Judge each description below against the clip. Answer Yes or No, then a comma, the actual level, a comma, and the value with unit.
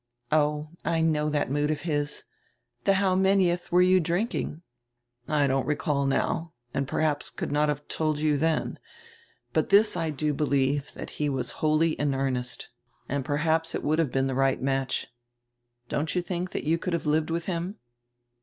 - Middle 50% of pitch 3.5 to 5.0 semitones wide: No, narrow, 2.6 semitones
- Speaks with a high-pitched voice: No, medium, 150 Hz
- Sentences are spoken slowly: No, average, 175 wpm